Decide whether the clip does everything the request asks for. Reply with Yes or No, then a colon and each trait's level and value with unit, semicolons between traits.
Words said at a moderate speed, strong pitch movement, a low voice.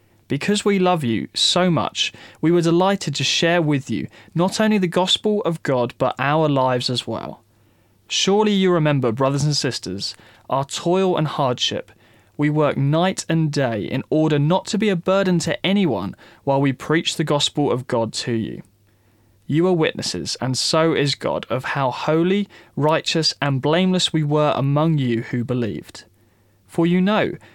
No: average, 170 wpm; wide, 6.5 semitones; medium, 150 Hz